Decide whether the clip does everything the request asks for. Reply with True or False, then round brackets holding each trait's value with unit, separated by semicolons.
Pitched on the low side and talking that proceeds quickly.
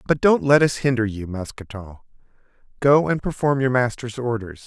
False (120 Hz; 165 wpm)